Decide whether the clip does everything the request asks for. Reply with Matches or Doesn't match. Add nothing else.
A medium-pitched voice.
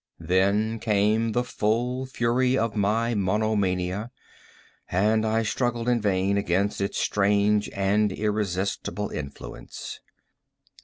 Doesn't match